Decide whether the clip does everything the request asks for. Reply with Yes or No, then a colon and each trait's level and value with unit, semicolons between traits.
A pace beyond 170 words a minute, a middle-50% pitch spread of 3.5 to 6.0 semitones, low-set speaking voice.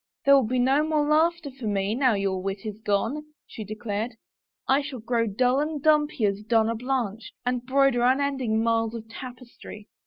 No: average, 195 wpm; average, 4.0 semitones; high, 245 Hz